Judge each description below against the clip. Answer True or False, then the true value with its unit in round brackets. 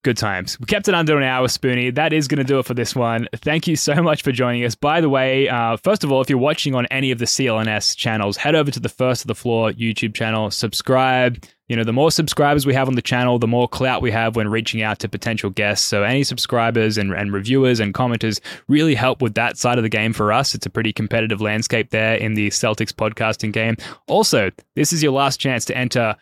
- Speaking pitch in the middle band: False (120 Hz)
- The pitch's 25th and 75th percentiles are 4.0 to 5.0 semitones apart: False (3.2 semitones)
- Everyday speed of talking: False (250 wpm)